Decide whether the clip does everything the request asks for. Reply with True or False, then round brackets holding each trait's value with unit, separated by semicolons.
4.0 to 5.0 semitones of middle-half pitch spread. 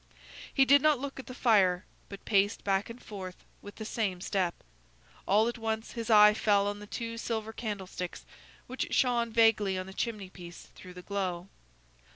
False (3.2 semitones)